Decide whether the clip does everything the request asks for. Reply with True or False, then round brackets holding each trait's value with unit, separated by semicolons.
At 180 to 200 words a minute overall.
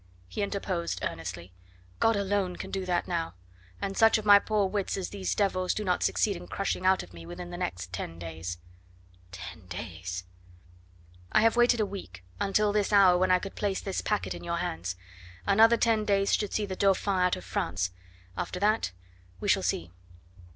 True (190 wpm)